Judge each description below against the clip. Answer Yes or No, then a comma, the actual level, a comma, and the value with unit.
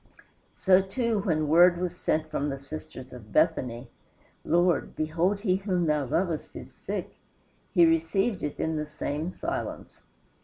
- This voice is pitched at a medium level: Yes, medium, 165 Hz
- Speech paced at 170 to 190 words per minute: No, average, 150 wpm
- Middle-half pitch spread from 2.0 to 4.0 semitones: Yes, average, 3.4 semitones